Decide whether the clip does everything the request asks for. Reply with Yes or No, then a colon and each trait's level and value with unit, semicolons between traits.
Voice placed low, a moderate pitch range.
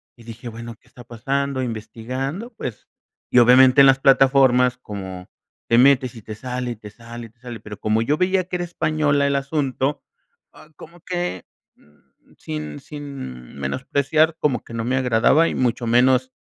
Yes: low, 125 Hz; average, 3.4 semitones